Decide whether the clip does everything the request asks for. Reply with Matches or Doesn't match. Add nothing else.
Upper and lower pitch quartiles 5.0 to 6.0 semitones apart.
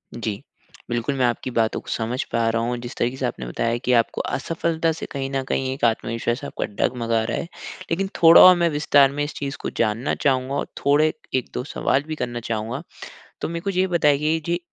Doesn't match